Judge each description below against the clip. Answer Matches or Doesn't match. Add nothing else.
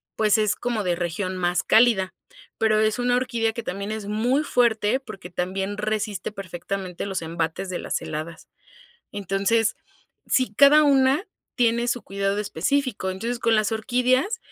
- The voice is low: Doesn't match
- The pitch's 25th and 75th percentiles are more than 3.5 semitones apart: Matches